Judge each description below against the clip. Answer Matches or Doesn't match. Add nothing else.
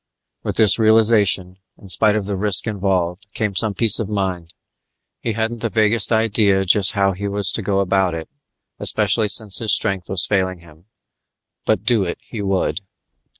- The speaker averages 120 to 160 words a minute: Doesn't match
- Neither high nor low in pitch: Doesn't match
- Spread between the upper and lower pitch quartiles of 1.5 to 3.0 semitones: Matches